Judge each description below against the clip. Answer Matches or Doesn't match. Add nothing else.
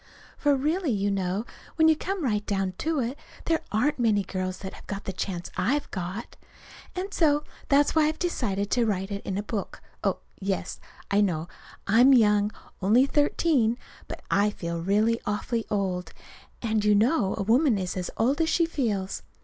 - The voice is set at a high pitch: Matches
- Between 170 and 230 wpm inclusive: Matches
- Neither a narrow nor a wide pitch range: Doesn't match